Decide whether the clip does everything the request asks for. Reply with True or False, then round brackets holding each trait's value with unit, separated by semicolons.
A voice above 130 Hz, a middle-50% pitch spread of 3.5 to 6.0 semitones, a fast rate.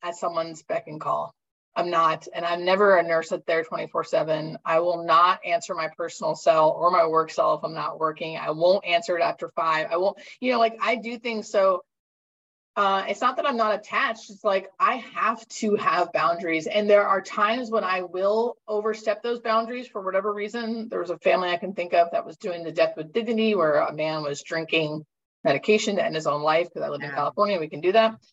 True (190 Hz; 5.2 semitones; 225 wpm)